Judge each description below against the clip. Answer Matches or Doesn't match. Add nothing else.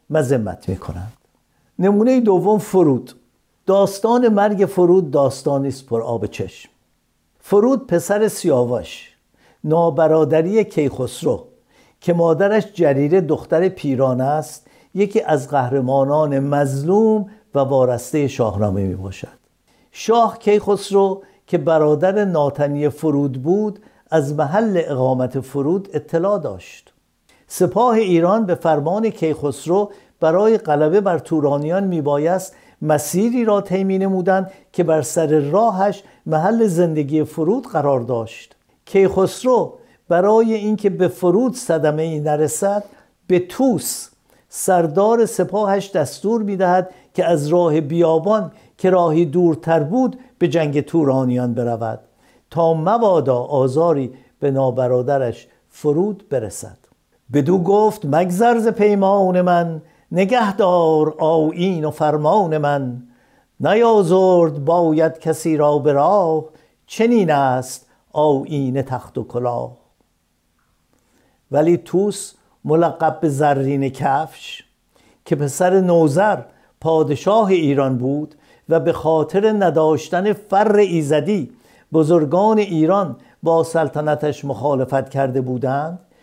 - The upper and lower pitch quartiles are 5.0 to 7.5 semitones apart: Matches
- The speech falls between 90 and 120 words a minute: Matches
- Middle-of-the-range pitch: Matches